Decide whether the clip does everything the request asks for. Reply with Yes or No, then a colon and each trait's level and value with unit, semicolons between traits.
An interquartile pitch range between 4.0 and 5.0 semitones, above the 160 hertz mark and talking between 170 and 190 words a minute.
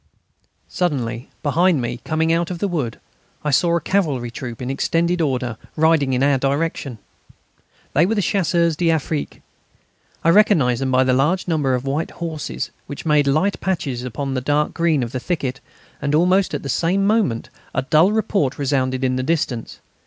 No: average, 4.6 semitones; medium, 150 Hz; average, 175 wpm